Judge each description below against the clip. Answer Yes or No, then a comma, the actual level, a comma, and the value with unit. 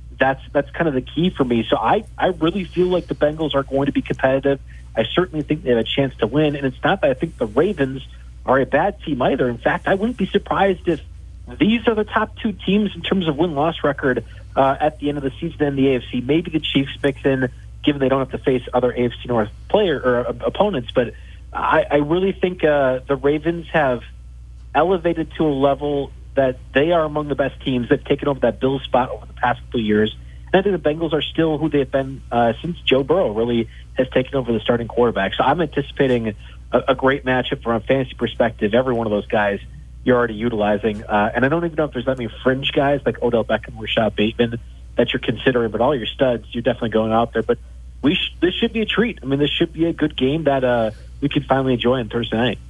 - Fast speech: Yes, fast, 245 wpm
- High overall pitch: No, low, 135 Hz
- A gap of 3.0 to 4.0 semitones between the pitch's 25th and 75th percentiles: No, average, 4.4 semitones